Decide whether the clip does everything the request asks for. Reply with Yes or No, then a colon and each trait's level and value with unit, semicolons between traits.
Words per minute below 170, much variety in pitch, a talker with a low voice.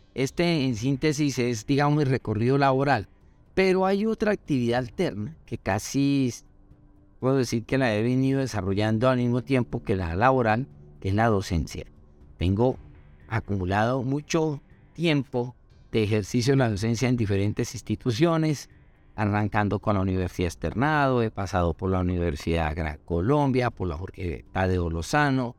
Yes: average, 150 wpm; wide, 5.9 semitones; low, 115 Hz